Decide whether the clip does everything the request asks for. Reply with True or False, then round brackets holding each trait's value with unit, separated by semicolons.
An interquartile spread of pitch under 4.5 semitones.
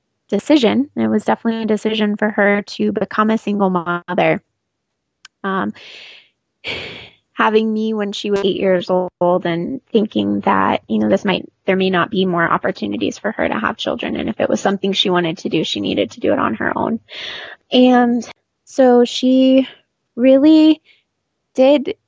False (5.0 semitones)